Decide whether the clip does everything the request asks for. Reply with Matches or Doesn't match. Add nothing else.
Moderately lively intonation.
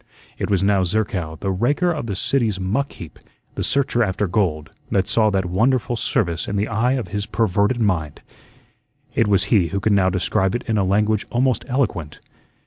Matches